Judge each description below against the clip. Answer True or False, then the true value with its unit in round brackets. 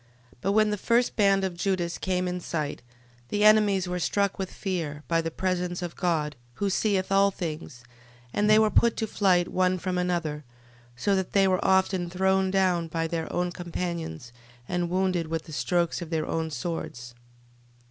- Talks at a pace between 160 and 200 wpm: True (185 wpm)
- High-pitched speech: False (180 Hz)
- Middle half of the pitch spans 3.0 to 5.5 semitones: False (2.6 semitones)